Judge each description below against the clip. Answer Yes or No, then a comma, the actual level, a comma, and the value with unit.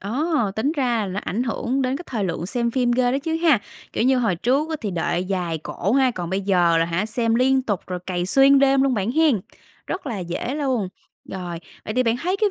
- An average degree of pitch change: No, wide, 6.0 semitones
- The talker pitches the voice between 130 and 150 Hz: No, high, 235 Hz